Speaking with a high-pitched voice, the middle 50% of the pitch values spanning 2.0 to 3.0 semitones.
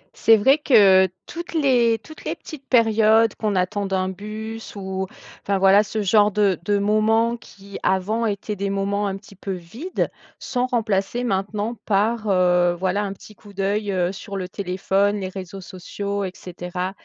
Yes: high, 200 Hz; narrow, 2.5 semitones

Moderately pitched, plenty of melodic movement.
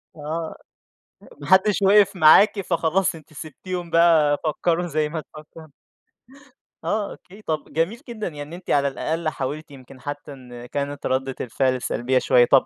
No: medium, 155 Hz; average, 3.8 semitones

